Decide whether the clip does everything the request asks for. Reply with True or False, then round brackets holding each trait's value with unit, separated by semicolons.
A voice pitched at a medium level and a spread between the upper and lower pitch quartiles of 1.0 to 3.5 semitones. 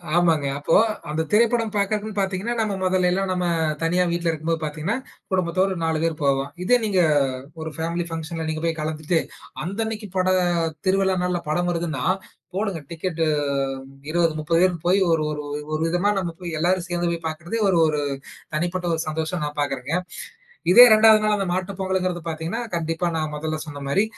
True (175 Hz; 2.9 semitones)